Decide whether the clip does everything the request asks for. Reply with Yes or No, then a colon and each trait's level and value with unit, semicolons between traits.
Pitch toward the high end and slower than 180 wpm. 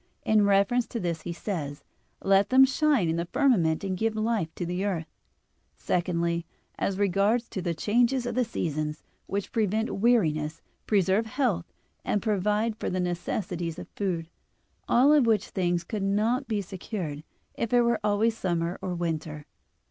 Yes: high, 195 Hz; average, 160 wpm